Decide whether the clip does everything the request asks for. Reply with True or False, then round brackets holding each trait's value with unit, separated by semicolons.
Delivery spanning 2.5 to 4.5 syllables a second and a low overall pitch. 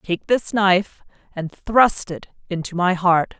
False (4.0 syllables/s; 185 Hz)